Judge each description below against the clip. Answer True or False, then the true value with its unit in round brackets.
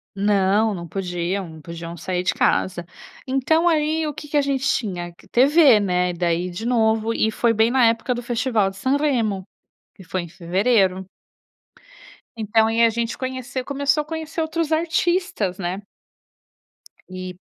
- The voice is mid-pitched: False (220 Hz)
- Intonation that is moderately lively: False (6.6 semitones)